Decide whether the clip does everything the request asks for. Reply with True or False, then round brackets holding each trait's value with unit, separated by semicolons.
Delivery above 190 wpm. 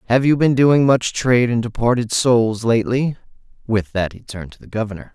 True (200 wpm)